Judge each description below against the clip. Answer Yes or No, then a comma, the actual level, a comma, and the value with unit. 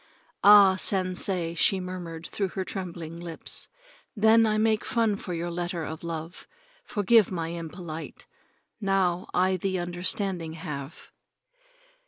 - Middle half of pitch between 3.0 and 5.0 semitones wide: No, narrow, 2.6 semitones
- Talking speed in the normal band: No, slow, 125 wpm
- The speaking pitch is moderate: Yes, medium, 180 Hz